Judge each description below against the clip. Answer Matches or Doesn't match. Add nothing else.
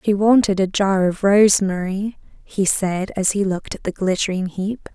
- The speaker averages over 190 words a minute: Doesn't match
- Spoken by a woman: Matches